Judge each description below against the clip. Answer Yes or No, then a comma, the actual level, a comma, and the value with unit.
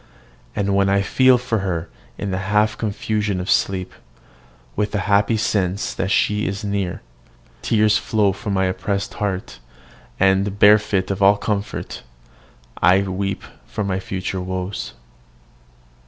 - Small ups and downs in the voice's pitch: Yes, narrow, 1.6 semitones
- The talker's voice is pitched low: Yes, low, 100 Hz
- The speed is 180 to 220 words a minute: No, average, 140 wpm